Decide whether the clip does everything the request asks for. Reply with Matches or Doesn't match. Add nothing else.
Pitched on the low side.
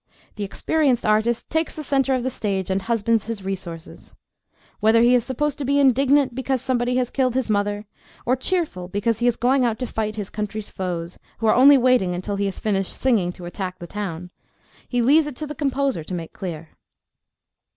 Doesn't match